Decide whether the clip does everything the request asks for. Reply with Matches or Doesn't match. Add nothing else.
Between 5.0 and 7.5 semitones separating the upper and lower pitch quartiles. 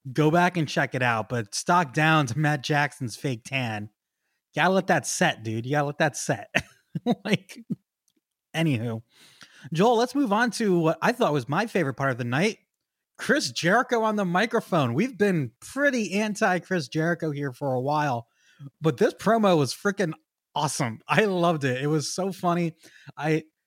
Matches